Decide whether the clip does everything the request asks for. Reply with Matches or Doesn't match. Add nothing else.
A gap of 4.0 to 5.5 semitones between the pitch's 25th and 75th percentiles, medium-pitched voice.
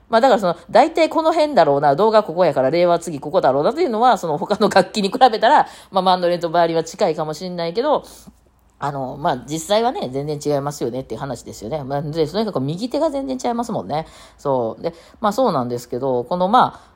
Doesn't match